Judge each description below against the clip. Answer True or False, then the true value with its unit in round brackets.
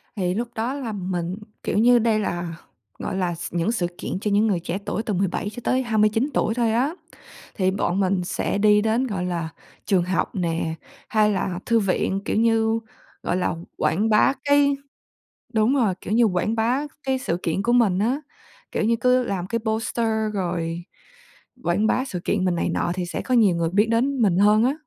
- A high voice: True (210 Hz)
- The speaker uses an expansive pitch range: False (4.3 semitones)